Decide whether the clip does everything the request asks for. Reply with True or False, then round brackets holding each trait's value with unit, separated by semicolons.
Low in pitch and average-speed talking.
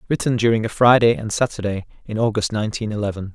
True (110 Hz; 180 wpm)